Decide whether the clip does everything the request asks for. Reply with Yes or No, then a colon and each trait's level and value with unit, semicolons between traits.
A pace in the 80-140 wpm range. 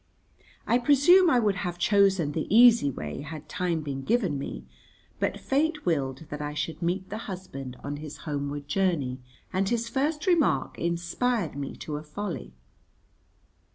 No: average, 155 wpm